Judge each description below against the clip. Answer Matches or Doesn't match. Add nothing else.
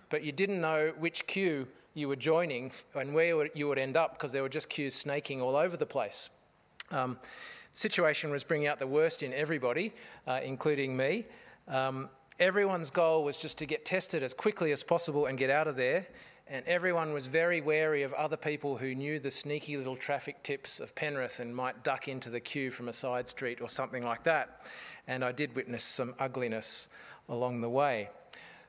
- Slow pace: Doesn't match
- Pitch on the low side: Doesn't match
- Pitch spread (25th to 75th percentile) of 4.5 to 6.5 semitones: Doesn't match